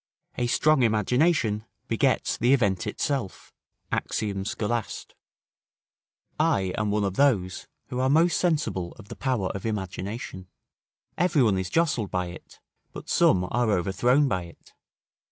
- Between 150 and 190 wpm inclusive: No, slow, 135 wpm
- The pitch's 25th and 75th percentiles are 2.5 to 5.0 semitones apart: No, wide, 5.5 semitones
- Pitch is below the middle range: Yes, low, 110 Hz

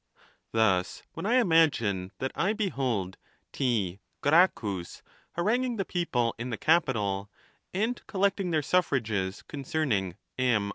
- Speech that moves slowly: Yes, slow, 130 wpm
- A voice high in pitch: No, low, 130 Hz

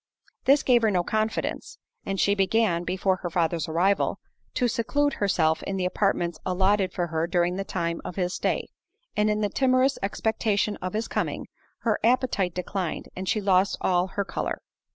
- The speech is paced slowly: No, average, 175 wpm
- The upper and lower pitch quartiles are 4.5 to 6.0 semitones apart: No, average, 3.3 semitones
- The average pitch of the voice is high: Yes, high, 195 Hz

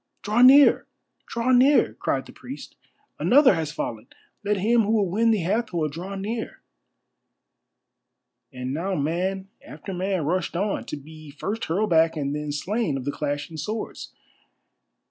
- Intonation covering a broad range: Yes, wide, 6.1 semitones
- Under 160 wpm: Yes, average, 150 wpm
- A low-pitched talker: No, medium, 185 Hz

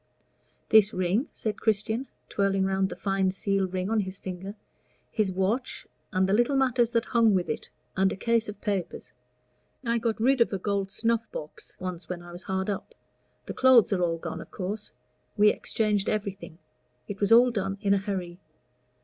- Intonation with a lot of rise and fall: No, average, 2.9 semitones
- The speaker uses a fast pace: No, average, 185 wpm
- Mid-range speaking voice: No, high, 200 Hz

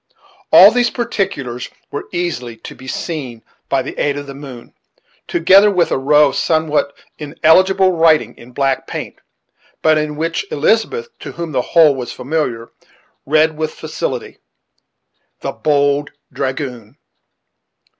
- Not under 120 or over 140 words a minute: Yes, slow, 135 wpm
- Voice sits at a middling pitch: Yes, medium, 150 Hz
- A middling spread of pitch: Yes, average, 3.7 semitones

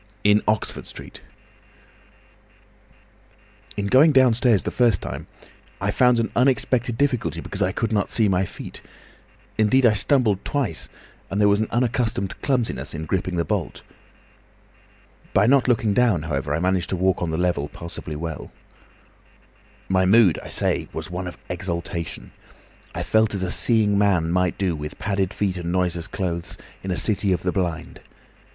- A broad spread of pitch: No, average, 4.3 semitones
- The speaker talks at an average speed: Yes, average, 160 wpm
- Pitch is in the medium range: No, very low, 95 Hz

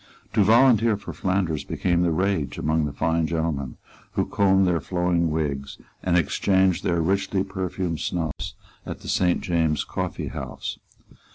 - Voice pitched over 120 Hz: No, very low, 90 Hz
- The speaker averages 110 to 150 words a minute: Yes, average, 145 wpm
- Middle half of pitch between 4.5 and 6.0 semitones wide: No, average, 3.0 semitones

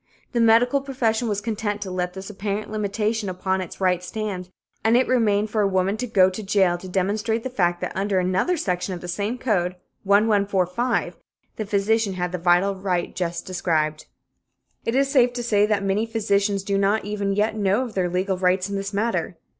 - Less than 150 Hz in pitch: No, high, 200 Hz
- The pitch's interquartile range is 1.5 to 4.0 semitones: Yes, average, 3.0 semitones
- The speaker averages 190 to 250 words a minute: Yes, average, 200 wpm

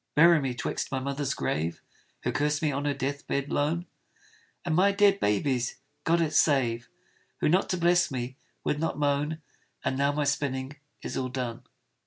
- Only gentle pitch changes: No, average, 3.2 semitones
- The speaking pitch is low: No, medium, 145 Hz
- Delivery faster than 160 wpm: Yes, average, 180 wpm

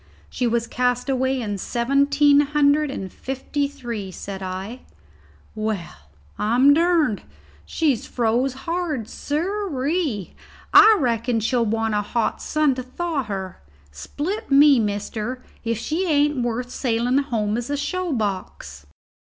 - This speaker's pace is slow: Yes, slow, 130 wpm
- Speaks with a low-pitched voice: No, very high, 250 Hz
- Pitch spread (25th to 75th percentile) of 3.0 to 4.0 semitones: No, average, 4.7 semitones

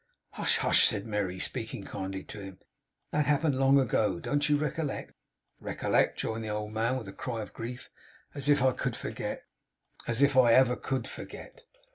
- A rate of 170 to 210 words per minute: Yes, average, 180 wpm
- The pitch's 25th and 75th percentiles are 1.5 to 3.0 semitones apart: No, average, 4.6 semitones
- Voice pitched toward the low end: Yes, low, 125 Hz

